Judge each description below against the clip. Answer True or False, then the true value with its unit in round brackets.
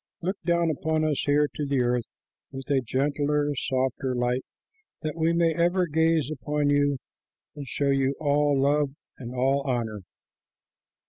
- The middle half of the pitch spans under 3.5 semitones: True (2.7 semitones)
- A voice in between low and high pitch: True (145 Hz)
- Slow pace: False (150 wpm)